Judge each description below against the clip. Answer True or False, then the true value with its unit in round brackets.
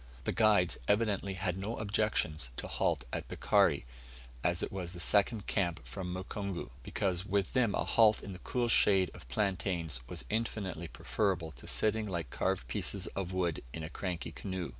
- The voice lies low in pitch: True (95 Hz)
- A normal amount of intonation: True (3.1 semitones)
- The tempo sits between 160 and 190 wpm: True (175 wpm)